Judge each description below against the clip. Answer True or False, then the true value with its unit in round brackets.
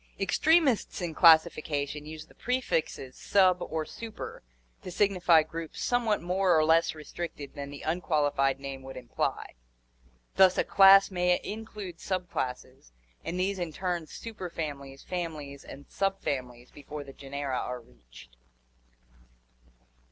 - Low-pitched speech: False (160 Hz)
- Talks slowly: True (130 wpm)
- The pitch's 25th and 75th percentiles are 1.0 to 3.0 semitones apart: False (4.8 semitones)